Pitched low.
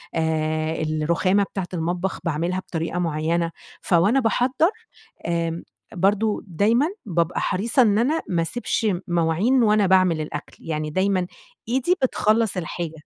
No: medium, 180 Hz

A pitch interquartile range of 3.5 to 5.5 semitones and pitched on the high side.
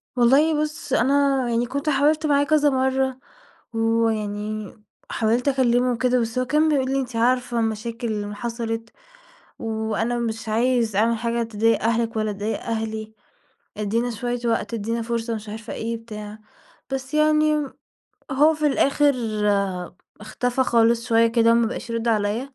No: average, 2.8 semitones; high, 235 Hz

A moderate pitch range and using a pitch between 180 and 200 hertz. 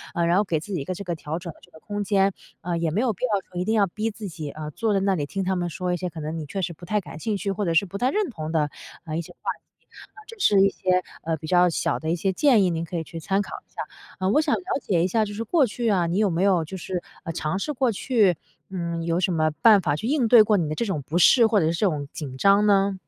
Yes: average, 3.9 semitones; medium, 185 Hz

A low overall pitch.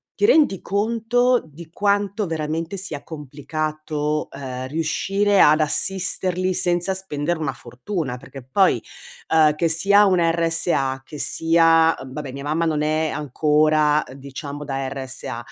No: medium, 155 Hz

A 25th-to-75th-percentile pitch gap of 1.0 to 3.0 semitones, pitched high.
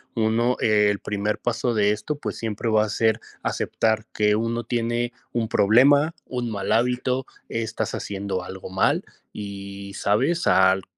No: narrow, 2.6 semitones; low, 110 Hz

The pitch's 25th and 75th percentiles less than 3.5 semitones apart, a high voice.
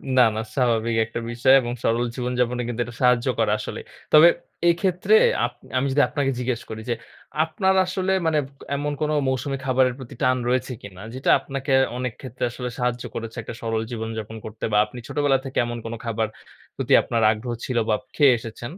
No: average, 2.8 semitones; low, 125 Hz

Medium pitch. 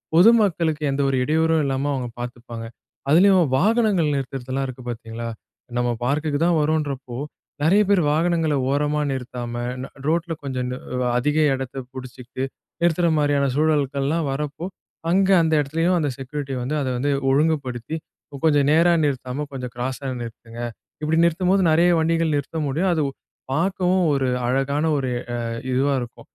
Yes: medium, 145 Hz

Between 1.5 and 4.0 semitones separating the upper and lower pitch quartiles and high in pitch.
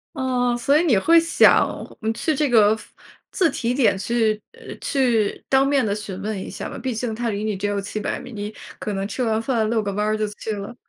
Yes: average, 3.7 semitones; high, 225 Hz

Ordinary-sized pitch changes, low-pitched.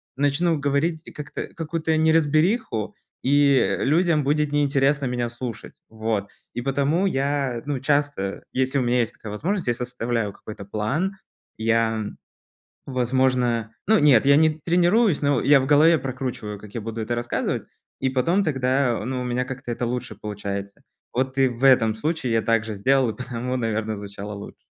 Yes: average, 4.1 semitones; low, 130 Hz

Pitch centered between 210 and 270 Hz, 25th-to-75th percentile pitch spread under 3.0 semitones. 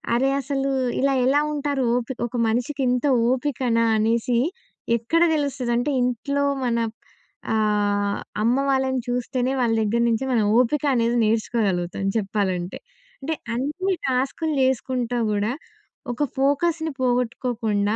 No: high, 245 Hz; average, 3.3 semitones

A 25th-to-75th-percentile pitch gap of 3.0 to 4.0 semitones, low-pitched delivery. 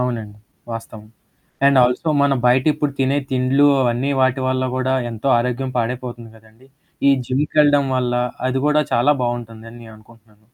No: narrow, 2.6 semitones; low, 125 Hz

